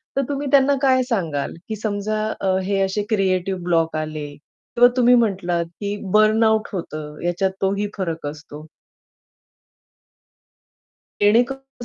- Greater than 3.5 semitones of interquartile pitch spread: Yes, average, 4.7 semitones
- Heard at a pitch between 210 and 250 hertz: No, high, 200 Hz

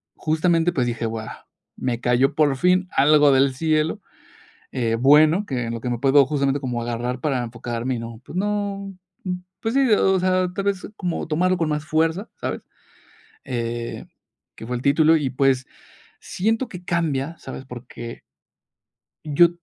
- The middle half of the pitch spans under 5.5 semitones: No, wide, 5.9 semitones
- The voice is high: No, medium, 145 Hz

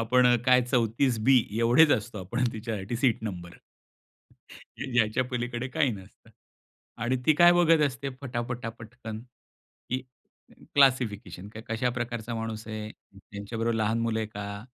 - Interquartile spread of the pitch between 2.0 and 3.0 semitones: Yes, average, 2.7 semitones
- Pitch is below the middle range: Yes, low, 115 Hz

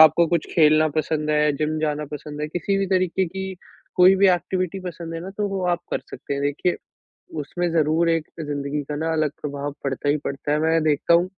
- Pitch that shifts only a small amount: No, average, 3.0 semitones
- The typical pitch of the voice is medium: Yes, medium, 160 Hz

